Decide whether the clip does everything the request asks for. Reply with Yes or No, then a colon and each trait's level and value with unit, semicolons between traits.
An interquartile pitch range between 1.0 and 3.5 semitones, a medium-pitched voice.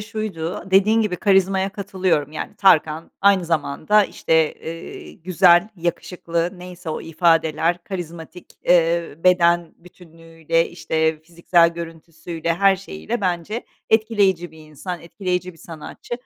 Yes: narrow, 2.5 semitones; medium, 170 Hz